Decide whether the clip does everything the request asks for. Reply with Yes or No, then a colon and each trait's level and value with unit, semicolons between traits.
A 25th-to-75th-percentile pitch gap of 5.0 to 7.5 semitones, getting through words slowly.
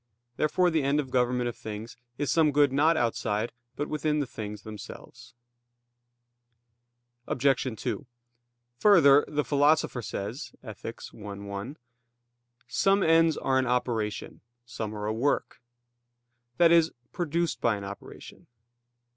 Yes: wide, 5.4 semitones; slow, 125 wpm